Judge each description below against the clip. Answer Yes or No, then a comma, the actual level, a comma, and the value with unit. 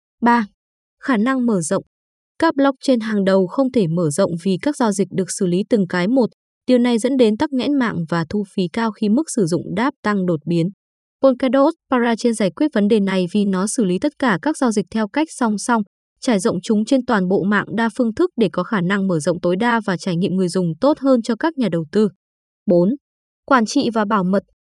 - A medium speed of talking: Yes, average, 240 wpm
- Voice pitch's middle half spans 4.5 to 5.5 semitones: Yes, average, 4.9 semitones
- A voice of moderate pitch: No, high, 220 Hz